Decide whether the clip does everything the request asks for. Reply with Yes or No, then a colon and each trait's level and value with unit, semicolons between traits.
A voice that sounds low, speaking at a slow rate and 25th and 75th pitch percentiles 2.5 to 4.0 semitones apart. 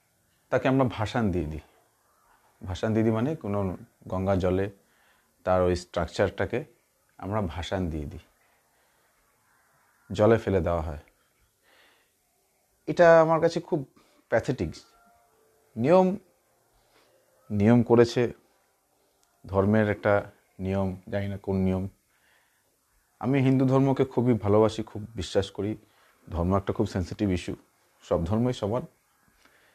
No: low, 105 Hz; slow, 110 wpm; average, 4.4 semitones